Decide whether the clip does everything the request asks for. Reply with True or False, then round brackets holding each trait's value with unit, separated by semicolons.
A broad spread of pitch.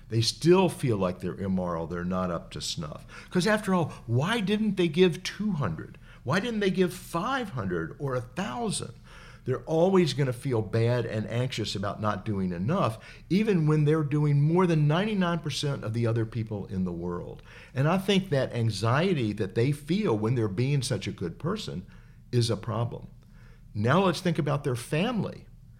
True (7.5 semitones)